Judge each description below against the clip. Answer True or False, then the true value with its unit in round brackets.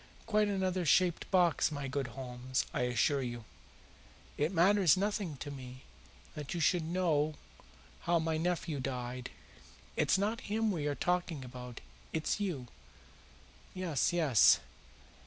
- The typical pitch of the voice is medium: True (155 Hz)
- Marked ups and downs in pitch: True (5.7 semitones)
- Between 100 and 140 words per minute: True (135 wpm)